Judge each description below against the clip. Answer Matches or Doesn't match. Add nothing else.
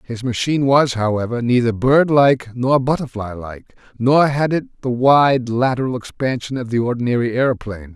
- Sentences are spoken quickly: Doesn't match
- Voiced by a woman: Doesn't match